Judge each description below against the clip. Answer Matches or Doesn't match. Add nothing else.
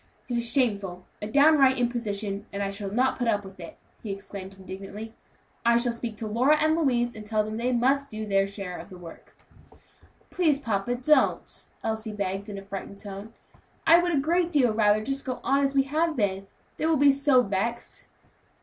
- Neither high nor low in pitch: Doesn't match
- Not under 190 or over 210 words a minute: Matches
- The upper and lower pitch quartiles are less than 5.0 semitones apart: Doesn't match